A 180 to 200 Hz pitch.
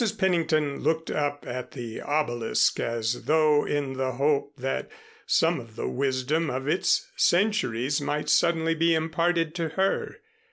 No: medium, 150 Hz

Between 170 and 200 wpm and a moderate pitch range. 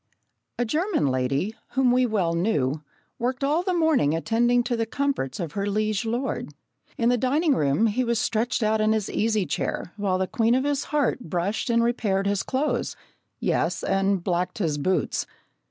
Yes: average, 180 wpm; average, 5.0 semitones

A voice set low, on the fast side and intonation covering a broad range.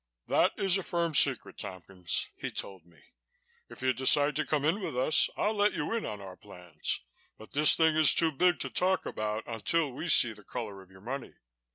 Yes: low, 130 Hz; fast, 210 wpm; wide, 7.6 semitones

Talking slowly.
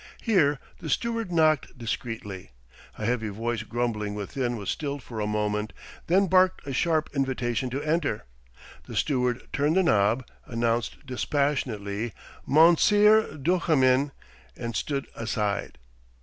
Yes: slow, 125 wpm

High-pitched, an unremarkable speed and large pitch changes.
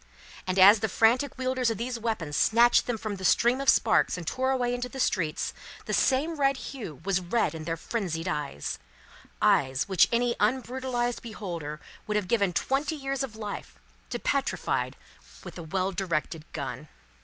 Yes: high, 220 Hz; average, 175 wpm; wide, 6.2 semitones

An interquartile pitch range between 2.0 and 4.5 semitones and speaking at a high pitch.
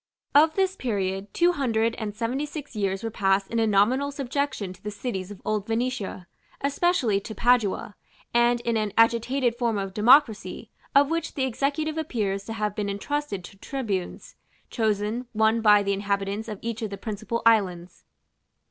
Yes: average, 4.1 semitones; high, 225 Hz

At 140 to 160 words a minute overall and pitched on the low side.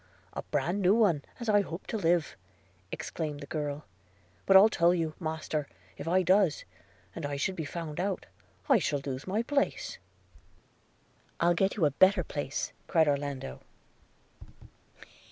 No: average, 155 wpm; medium, 165 Hz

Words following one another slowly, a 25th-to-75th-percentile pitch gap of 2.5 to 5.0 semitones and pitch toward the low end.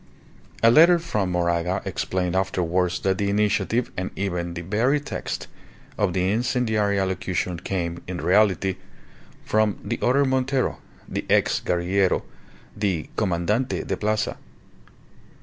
Yes: slow, 125 wpm; average, 3.5 semitones; very low, 95 Hz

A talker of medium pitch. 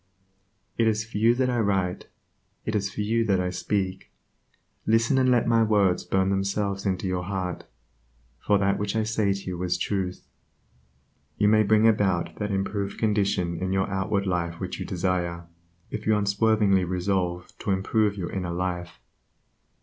No: low, 100 Hz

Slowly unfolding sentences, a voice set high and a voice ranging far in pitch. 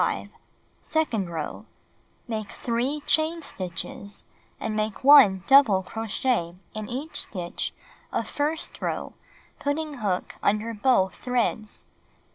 Yes: slow, 105 wpm; high, 225 Hz; wide, 6.0 semitones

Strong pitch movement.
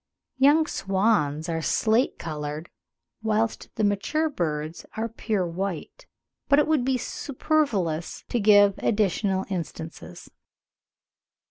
Yes: wide, 6.2 semitones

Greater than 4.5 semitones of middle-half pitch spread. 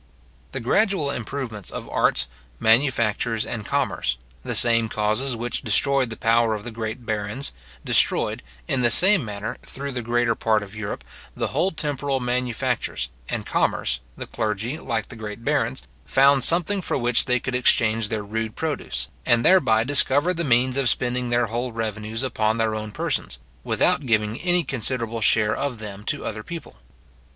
No: average, 3.6 semitones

